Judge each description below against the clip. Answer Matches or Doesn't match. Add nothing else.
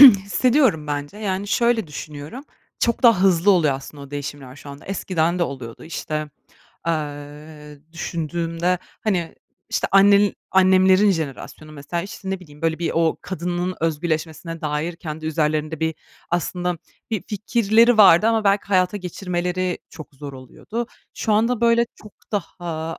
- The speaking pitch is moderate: Matches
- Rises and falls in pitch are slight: Doesn't match